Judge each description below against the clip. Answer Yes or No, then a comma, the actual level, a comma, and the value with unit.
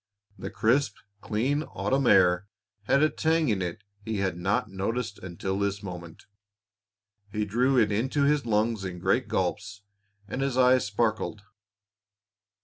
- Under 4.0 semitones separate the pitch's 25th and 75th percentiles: No, average, 4.8 semitones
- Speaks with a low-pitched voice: Yes, low, 105 Hz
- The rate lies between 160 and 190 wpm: No, average, 140 wpm